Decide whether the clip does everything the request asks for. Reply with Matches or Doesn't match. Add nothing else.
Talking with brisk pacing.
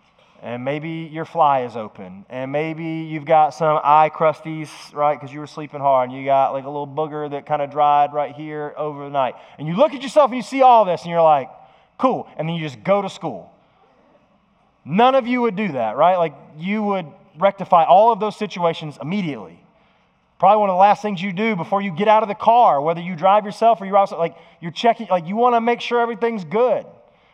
Matches